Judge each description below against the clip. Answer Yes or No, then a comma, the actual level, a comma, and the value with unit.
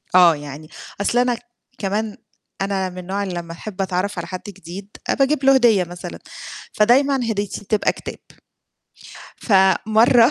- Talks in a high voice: Yes, high, 200 Hz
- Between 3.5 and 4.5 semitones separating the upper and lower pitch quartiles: Yes, average, 4.0 semitones